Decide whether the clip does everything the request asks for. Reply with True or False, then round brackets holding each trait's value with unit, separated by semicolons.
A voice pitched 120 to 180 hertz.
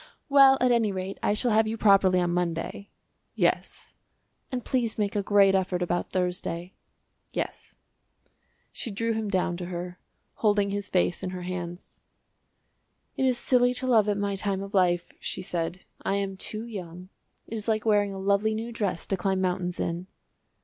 False (195 Hz)